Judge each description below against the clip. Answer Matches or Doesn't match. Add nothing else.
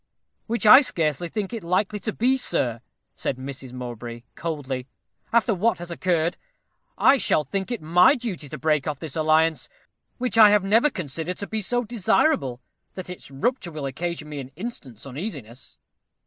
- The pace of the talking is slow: Doesn't match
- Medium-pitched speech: Matches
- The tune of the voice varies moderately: Doesn't match